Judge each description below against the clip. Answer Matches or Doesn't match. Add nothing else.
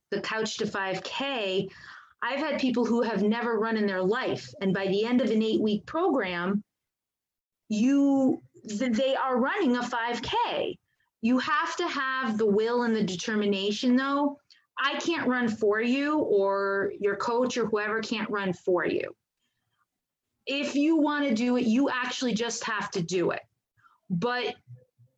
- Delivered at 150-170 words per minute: Matches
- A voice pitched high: Matches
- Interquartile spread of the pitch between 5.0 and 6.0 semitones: Doesn't match